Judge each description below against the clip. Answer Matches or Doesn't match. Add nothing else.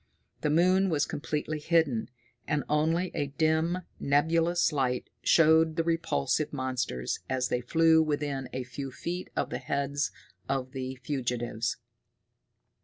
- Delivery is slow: Matches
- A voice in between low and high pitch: Matches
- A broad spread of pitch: Doesn't match